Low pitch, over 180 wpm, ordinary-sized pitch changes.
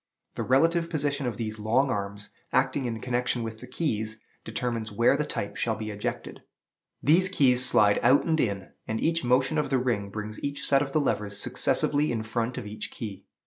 Yes: low, 120 Hz; average, 195 wpm; average, 4.5 semitones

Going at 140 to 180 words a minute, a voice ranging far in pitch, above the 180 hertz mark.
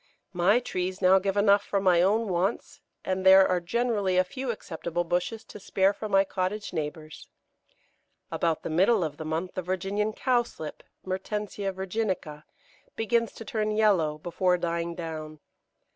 No: average, 155 wpm; average, 3.4 semitones; high, 190 Hz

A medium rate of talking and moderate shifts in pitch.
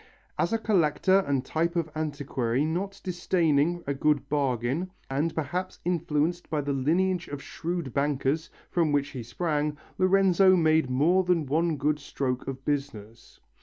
Yes: average, 150 wpm; average, 3.7 semitones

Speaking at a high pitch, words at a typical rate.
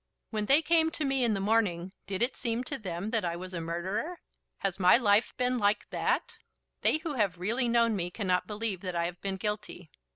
No: high, 210 Hz; fast, 220 wpm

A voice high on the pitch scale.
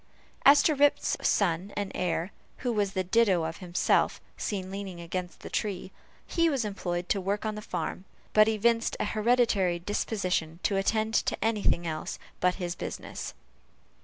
Yes: high, 195 Hz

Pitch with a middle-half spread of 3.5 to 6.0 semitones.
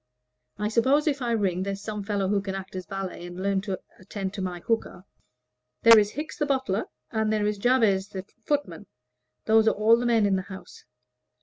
No: average, 3.0 semitones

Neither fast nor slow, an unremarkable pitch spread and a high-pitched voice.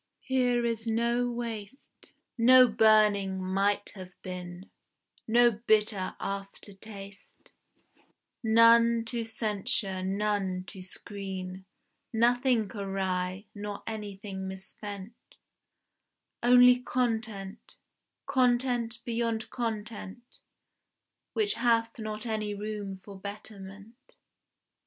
No: slow, 85 wpm; average, 3.1 semitones; high, 215 Hz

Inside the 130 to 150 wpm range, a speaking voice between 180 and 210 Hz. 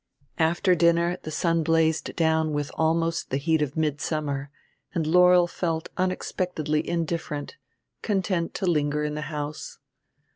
No: slow, 135 wpm; medium, 160 Hz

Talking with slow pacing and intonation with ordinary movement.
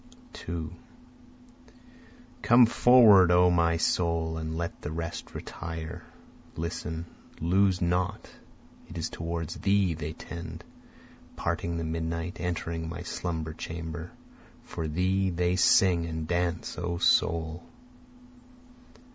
No: slow, 110 wpm; narrow, 1.5 semitones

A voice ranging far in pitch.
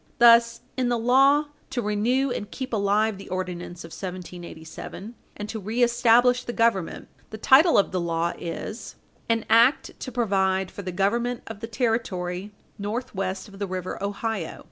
No: average, 4.1 semitones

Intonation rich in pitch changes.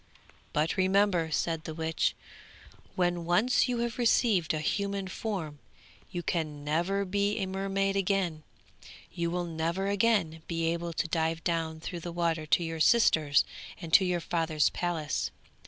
No: average, 3.4 semitones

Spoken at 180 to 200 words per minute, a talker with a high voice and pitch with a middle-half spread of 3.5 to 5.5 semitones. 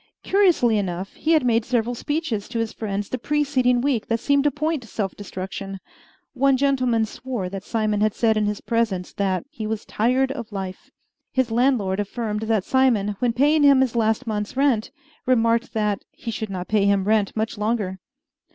Yes: average, 190 wpm; high, 225 Hz; average, 3.8 semitones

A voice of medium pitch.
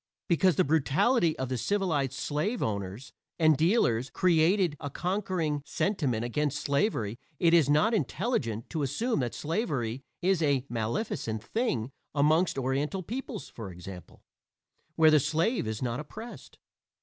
Yes: medium, 150 Hz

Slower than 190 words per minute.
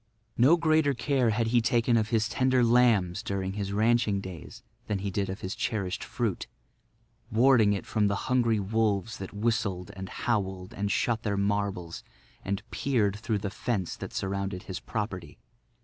Yes: average, 165 wpm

